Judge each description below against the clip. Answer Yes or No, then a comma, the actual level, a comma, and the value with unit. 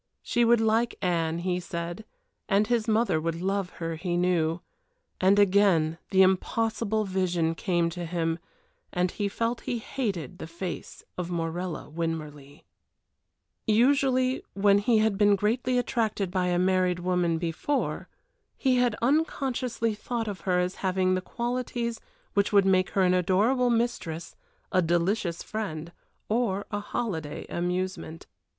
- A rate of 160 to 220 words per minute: No, average, 145 wpm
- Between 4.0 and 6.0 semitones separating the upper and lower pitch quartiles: Yes, average, 4.4 semitones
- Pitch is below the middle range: No, high, 190 Hz